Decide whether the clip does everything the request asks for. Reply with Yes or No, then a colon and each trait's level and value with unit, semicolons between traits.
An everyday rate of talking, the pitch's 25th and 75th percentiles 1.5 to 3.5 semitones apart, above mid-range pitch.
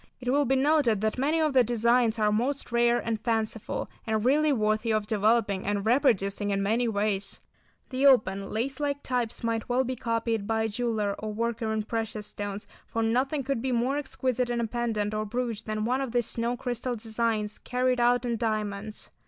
Yes: average, 195 wpm; average, 2.7 semitones; high, 230 Hz